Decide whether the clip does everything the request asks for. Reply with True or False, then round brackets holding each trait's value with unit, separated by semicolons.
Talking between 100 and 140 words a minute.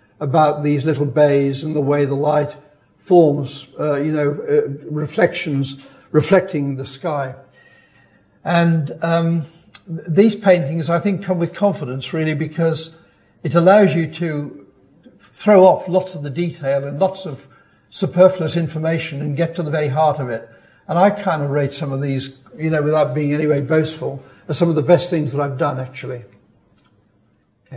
False (160 wpm)